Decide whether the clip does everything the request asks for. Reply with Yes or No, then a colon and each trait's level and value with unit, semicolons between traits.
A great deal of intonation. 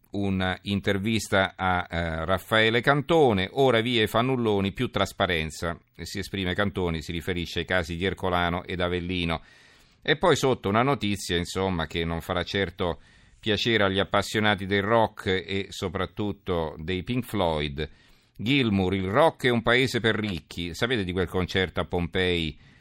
No: average, 3.4 semitones